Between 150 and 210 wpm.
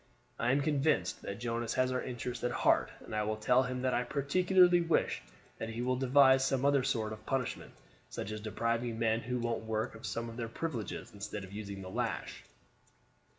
Yes: average, 200 wpm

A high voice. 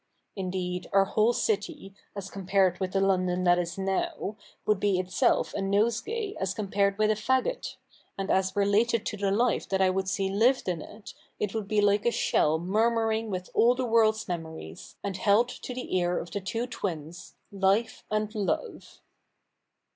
Yes: high, 200 Hz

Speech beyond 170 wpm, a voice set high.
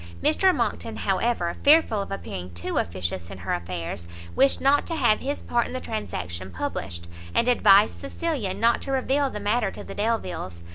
Yes: average, 180 wpm; high, 210 Hz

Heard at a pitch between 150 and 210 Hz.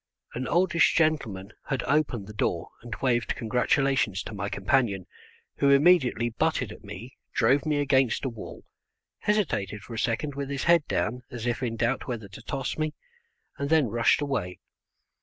No: low, 125 Hz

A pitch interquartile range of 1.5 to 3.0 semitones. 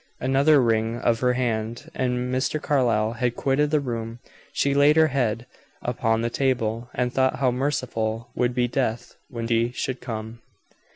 Yes: narrow, 2.6 semitones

